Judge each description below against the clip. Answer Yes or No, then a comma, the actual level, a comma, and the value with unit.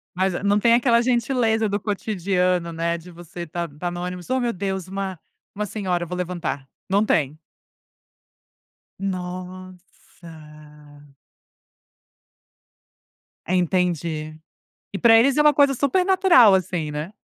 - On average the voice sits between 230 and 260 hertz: No, medium, 185 Hz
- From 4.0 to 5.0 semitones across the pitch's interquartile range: Yes, average, 4.3 semitones